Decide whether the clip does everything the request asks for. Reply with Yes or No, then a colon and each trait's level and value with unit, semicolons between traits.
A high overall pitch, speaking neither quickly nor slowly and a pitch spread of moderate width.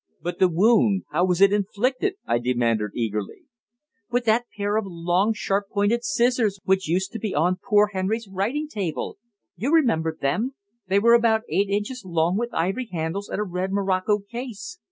Yes: high, 200 Hz; average, 175 wpm; average, 4.1 semitones